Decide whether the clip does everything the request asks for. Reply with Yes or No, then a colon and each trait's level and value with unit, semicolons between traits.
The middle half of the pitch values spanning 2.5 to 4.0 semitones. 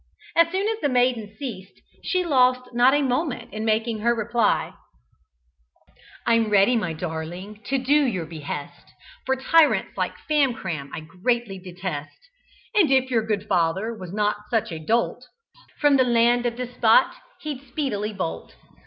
No: average, 5.2 semitones